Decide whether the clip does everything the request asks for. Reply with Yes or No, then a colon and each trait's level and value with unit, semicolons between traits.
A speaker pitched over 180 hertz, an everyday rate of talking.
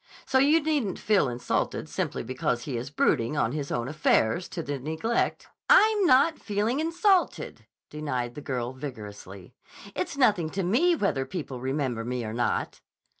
No: medium, 150 Hz; average, 160 wpm